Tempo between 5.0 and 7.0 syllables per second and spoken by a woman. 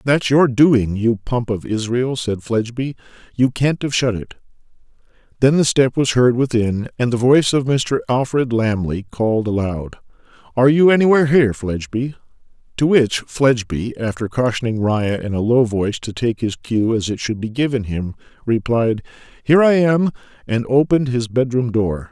No: 5.1 syllables/s; male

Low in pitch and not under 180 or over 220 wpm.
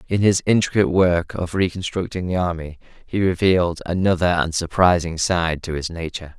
No: very low, 90 Hz; average, 160 wpm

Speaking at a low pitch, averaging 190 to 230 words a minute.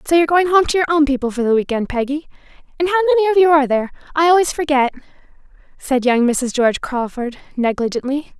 No: very high, 290 Hz; average, 195 wpm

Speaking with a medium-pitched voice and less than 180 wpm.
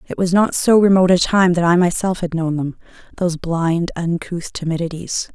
No: medium, 175 Hz; average, 190 wpm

